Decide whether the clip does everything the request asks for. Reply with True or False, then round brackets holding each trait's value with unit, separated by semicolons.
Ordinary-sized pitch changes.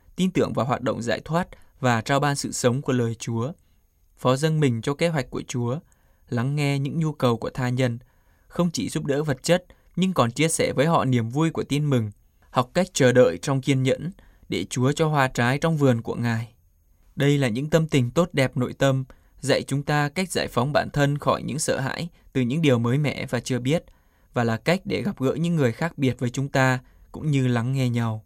True (3.6 semitones)